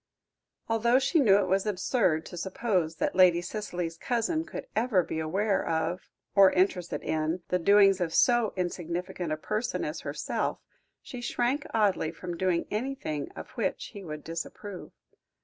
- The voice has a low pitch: No, high, 190 Hz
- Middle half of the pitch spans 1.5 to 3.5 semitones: No, average, 4.5 semitones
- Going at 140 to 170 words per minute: Yes, average, 155 wpm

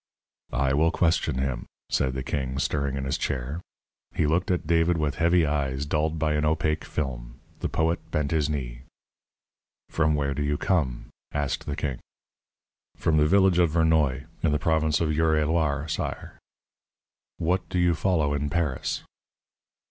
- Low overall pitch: Yes, very low, 75 Hz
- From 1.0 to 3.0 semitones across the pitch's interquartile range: Yes, narrow, 2.6 semitones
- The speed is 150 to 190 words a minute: Yes, average, 165 wpm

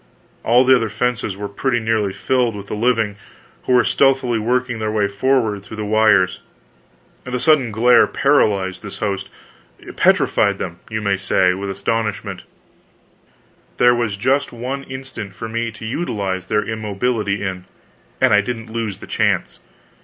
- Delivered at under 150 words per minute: No, average, 155 wpm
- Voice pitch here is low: Yes, low, 110 Hz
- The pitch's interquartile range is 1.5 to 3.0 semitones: No, average, 3.5 semitones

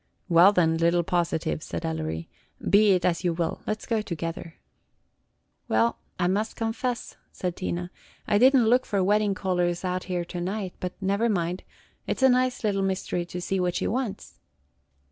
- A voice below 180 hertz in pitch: No, medium, 185 Hz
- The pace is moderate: Yes, average, 185 wpm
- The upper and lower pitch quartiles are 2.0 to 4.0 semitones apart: Yes, average, 3.5 semitones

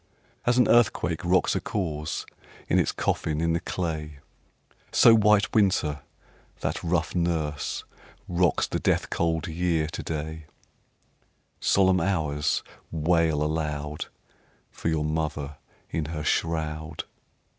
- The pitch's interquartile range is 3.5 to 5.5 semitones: No, narrow, 2.4 semitones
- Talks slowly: Yes, slow, 125 wpm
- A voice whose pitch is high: No, very low, 80 Hz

